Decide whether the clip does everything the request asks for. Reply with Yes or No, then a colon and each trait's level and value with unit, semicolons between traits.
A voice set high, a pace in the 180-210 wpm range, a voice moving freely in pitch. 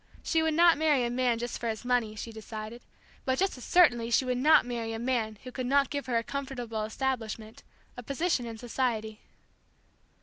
No: high, 245 Hz; average, 200 wpm; average, 3.0 semitones